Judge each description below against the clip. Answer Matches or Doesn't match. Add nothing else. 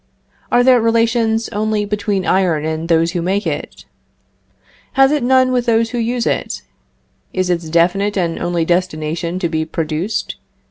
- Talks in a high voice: Matches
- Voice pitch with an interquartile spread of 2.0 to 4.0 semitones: Doesn't match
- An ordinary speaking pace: Matches